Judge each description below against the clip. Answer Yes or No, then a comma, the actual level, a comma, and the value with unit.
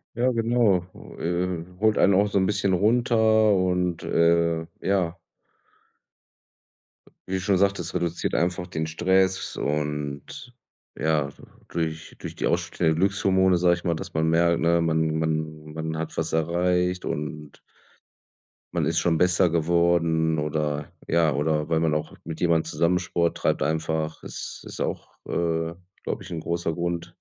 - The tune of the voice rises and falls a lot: No, narrow, 2.4 semitones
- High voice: No, very low, 85 Hz